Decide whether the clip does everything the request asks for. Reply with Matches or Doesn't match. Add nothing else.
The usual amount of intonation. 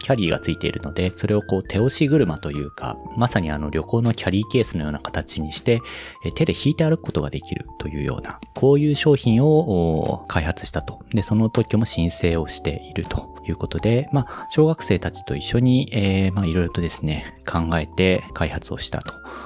Doesn't match